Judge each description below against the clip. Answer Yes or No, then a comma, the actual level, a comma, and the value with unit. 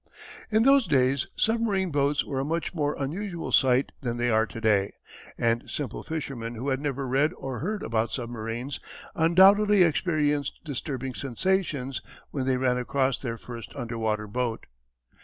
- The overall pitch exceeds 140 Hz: No, low, 135 Hz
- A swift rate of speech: No, average, 155 wpm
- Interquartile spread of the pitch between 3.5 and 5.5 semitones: Yes, average, 5.1 semitones